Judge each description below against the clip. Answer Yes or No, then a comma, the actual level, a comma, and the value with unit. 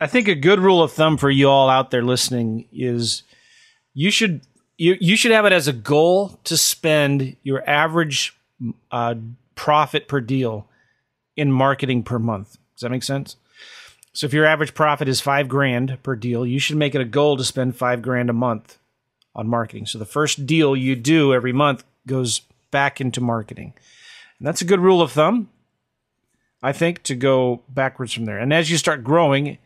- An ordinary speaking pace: Yes, average, 190 wpm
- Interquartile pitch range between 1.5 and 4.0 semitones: Yes, average, 3.7 semitones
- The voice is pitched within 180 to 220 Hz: No, low, 135 Hz